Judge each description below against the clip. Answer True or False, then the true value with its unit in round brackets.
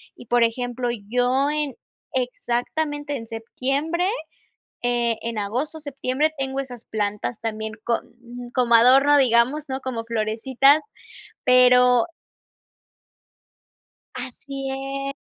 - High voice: True (250 Hz)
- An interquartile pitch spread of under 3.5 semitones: True (2.8 semitones)